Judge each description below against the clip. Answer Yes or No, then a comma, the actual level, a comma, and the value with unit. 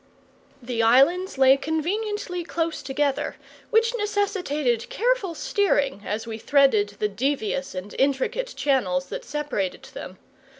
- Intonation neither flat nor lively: No, wide, 8.1 semitones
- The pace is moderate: No, slow, 120 wpm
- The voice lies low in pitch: No, very high, 280 Hz